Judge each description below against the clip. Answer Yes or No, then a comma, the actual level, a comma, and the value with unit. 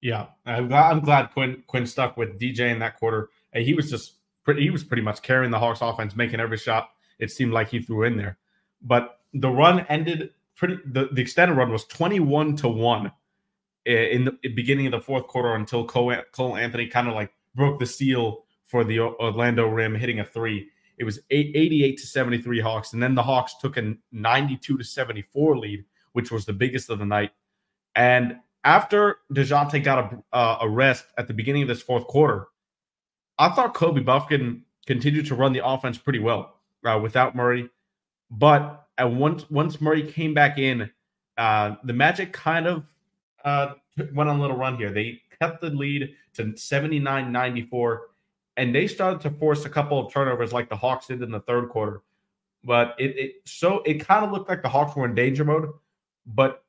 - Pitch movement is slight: No, average, 3.9 semitones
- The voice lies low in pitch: Yes, low, 130 Hz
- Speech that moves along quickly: No, average, 195 wpm